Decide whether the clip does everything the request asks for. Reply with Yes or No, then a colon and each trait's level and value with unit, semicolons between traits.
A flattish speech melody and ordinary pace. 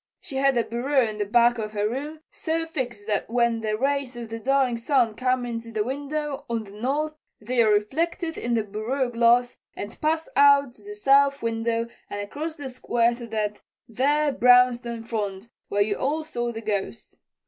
No: average, 3.7 semitones; average, 190 wpm